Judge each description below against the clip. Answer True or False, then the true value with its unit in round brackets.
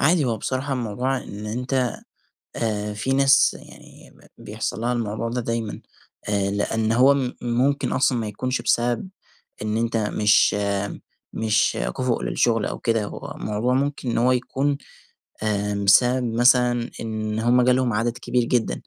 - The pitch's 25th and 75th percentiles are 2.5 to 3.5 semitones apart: True (2.8 semitones)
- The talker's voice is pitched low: True (120 Hz)